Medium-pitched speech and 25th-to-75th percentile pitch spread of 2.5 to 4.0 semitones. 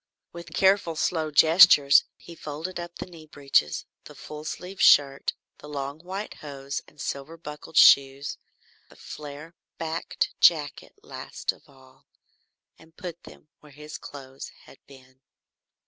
Yes: medium, 150 Hz; average, 3.0 semitones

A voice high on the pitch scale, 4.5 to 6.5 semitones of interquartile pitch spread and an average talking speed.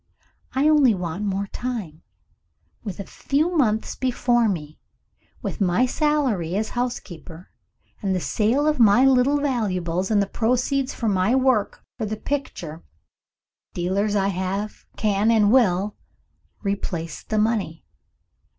No: high, 210 Hz; average, 5.0 semitones; slow, 130 wpm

